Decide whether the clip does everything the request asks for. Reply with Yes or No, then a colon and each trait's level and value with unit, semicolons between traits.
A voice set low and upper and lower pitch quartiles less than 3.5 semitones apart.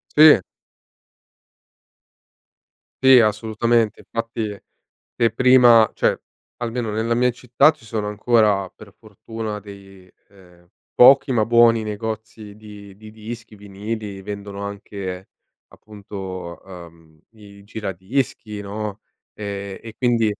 Yes: low, 105 Hz; narrow, 2.5 semitones